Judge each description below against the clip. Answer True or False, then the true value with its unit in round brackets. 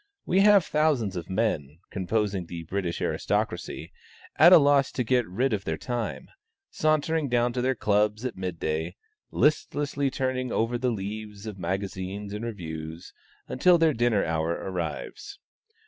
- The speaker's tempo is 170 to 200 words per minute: False (150 wpm)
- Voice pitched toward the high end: False (110 Hz)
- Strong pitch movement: True (5.9 semitones)